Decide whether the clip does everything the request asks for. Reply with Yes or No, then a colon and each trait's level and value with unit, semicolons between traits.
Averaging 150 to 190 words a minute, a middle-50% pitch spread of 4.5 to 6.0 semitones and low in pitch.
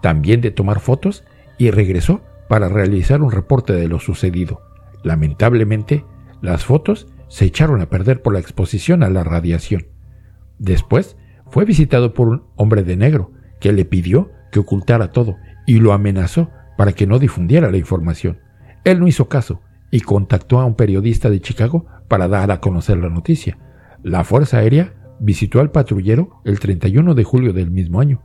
Yes: average, 170 wpm; average, 4.9 semitones; low, 105 Hz